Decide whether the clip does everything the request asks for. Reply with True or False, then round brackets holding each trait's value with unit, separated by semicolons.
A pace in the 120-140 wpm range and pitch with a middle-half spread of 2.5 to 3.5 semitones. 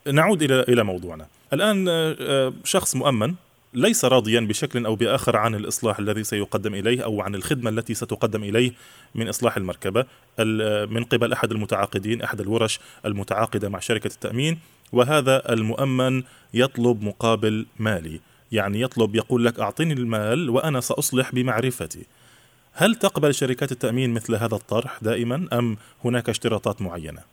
True (135 wpm; 3.0 semitones)